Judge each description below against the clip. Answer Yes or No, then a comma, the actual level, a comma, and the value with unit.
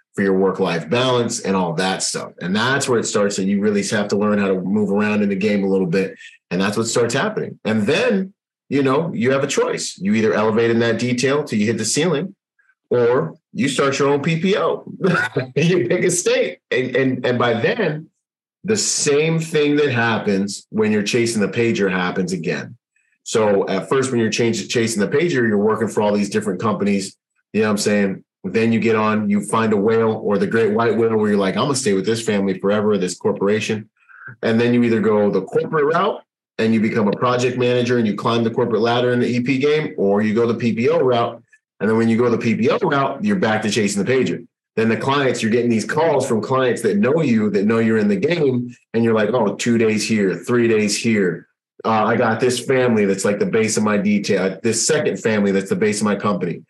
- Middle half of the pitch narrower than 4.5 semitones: No, wide, 5.5 semitones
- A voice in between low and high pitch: No, low, 115 Hz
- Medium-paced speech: No, fast, 235 wpm